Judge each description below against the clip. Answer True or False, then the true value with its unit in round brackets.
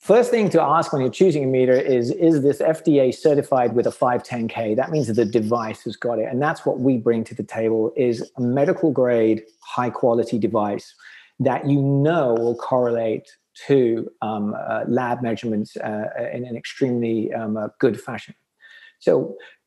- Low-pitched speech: True (120 Hz)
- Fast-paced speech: False (175 wpm)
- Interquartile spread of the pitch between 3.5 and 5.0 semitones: True (3.9 semitones)